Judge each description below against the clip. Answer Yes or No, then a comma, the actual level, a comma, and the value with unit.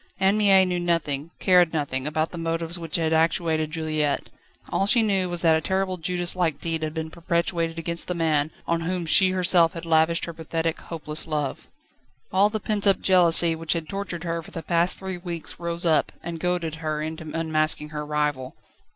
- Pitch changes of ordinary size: No, narrow, 2.0 semitones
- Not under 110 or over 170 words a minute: No, average, 195 wpm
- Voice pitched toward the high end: No, medium, 165 Hz